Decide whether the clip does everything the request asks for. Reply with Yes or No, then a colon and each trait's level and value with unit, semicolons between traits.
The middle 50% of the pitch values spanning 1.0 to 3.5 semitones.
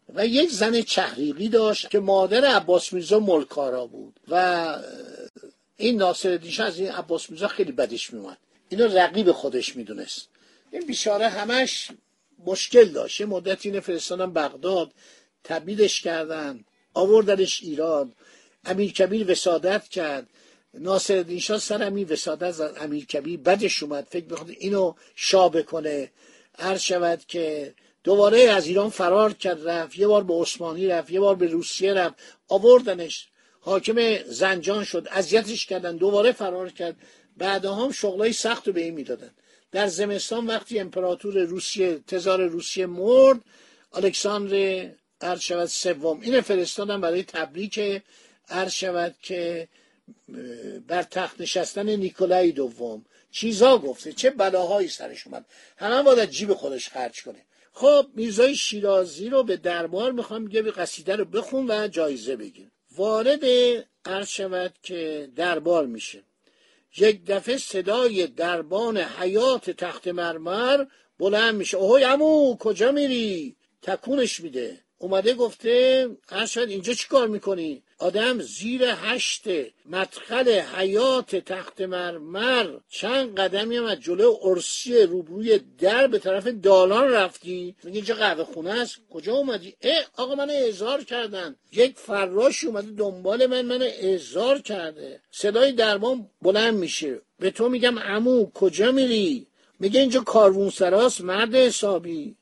No: average, 4.6 semitones